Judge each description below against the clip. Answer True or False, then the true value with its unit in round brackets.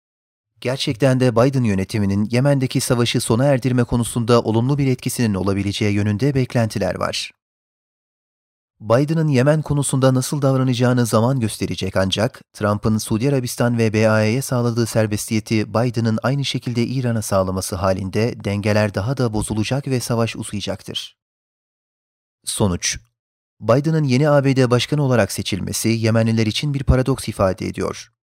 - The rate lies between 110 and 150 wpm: True (120 wpm)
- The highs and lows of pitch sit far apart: False (3.5 semitones)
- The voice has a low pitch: True (115 Hz)